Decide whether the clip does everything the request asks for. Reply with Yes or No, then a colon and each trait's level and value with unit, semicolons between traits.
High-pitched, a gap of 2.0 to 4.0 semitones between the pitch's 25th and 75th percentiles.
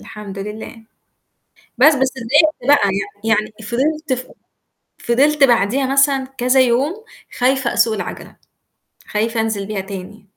No: high, 245 Hz; average, 4.4 semitones